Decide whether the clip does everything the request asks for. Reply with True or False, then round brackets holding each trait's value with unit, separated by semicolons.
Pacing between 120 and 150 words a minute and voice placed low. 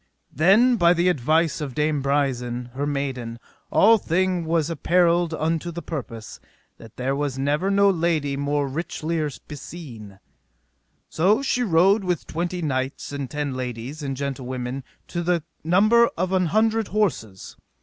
False (145 wpm; 155 Hz)